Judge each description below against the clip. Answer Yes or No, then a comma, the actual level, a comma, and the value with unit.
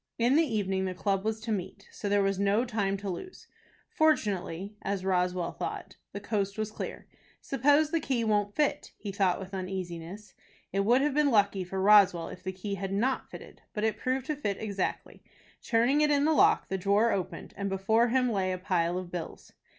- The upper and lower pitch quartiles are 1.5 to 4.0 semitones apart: Yes, average, 3.6 semitones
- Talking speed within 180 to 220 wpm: Yes, fast, 205 wpm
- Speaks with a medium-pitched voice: No, high, 200 Hz